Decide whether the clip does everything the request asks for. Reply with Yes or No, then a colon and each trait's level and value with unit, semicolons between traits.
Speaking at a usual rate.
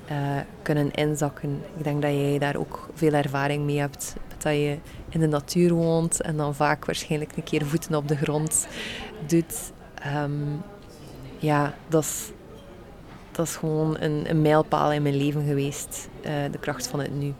Yes: average, 165 wpm